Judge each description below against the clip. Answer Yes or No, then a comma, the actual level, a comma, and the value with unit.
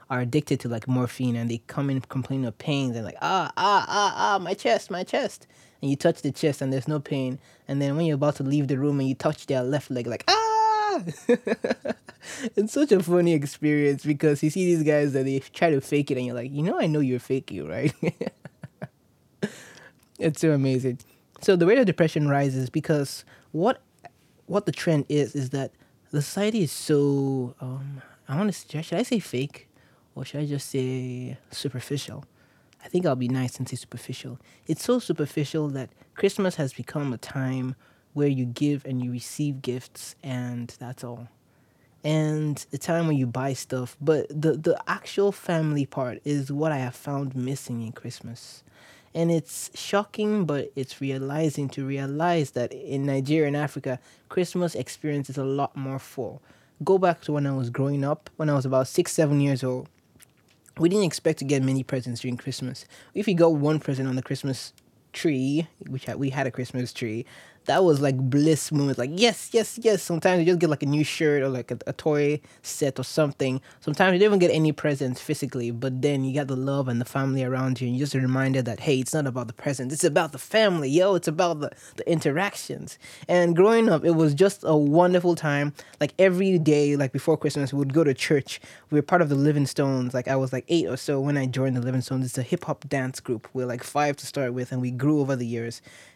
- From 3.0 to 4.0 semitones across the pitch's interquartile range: Yes, average, 3.3 semitones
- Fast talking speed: Yes, fast, 215 wpm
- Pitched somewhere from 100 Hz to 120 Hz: No, medium, 140 Hz